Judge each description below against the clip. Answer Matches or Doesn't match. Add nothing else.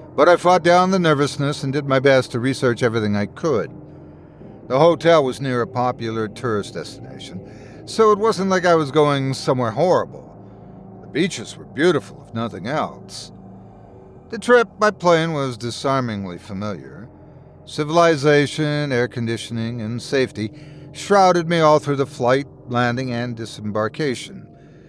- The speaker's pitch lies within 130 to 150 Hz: Matches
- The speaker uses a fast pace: Doesn't match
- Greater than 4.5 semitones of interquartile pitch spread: Matches